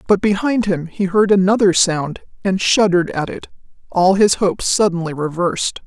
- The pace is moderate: Yes, average, 165 wpm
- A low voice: No, high, 190 Hz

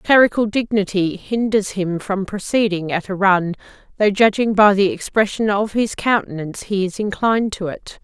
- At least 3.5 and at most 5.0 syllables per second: Yes, 4.9 syllables/s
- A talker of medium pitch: No, high, 200 Hz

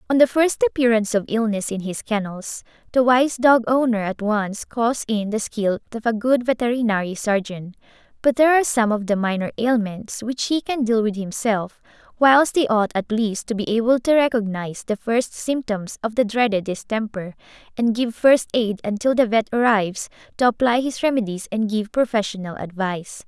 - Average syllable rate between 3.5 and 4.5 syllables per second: No, 5.1 syllables/s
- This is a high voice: Yes, high, 225 Hz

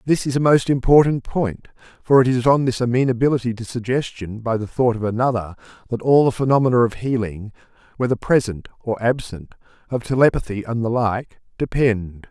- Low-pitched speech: Yes, low, 120 Hz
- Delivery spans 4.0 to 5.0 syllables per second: No, 5.5 syllables/s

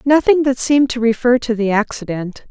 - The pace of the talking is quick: No, average, 190 wpm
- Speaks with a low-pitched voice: No, high, 240 Hz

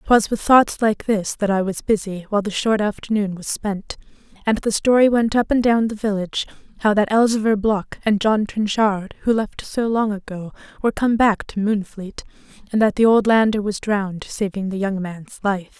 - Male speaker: No, female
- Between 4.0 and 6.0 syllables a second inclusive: Yes, 5.0 syllables/s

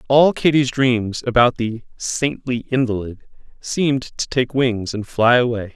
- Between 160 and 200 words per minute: No, average, 145 wpm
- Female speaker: No, male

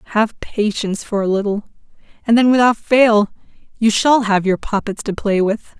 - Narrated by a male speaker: No, female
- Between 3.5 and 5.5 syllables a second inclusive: Yes, 5.0 syllables/s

